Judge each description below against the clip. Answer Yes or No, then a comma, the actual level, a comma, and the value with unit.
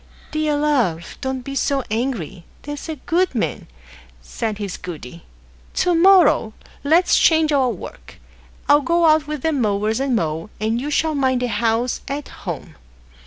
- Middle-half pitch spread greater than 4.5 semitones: Yes, wide, 5.6 semitones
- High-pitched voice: Yes, very high, 265 Hz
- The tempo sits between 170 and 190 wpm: No, average, 160 wpm